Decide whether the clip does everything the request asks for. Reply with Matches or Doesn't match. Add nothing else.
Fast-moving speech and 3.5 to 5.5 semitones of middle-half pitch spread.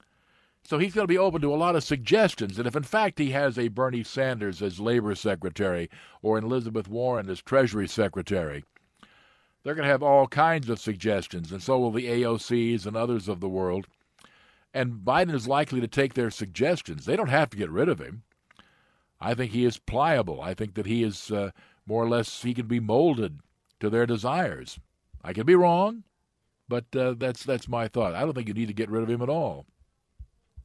Matches